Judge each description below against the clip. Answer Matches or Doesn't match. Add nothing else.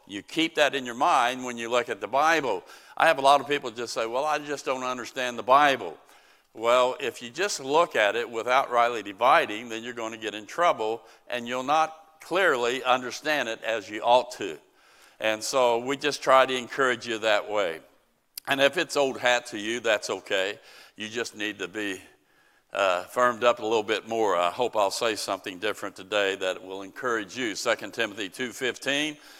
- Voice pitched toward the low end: Matches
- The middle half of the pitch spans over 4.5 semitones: Doesn't match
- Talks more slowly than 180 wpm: Doesn't match